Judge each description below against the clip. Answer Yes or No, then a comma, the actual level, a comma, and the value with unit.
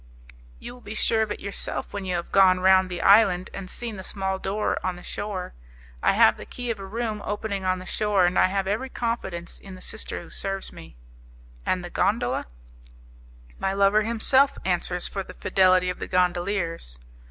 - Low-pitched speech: No, high, 195 Hz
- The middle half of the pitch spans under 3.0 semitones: Yes, narrow, 2.4 semitones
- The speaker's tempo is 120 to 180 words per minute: No, average, 200 wpm